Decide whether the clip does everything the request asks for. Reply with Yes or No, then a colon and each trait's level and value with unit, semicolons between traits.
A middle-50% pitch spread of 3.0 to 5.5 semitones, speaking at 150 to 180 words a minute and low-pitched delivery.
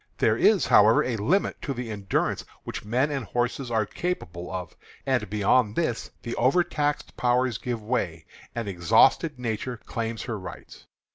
Yes: average, 3.6 semitones; average, 155 wpm; low, 120 Hz